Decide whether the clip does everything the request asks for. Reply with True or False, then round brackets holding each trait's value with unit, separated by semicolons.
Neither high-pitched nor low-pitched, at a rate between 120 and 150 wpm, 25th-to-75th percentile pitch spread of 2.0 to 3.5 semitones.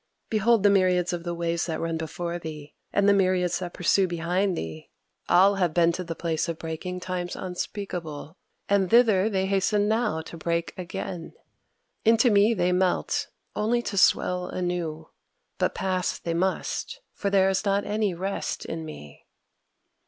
False (180 Hz; 165 wpm; 2.9 semitones)